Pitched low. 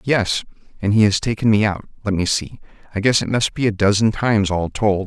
Yes: low, 105 Hz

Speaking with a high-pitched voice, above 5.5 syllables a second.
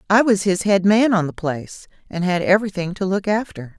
Yes: high, 195 Hz; 5.7 syllables/s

